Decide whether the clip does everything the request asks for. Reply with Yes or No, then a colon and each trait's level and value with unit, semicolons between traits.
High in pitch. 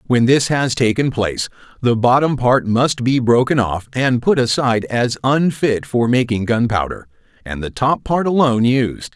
No: low, 125 Hz